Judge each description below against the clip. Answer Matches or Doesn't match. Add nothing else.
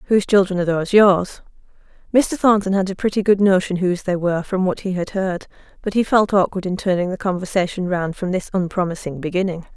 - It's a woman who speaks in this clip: Matches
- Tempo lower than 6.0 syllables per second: Doesn't match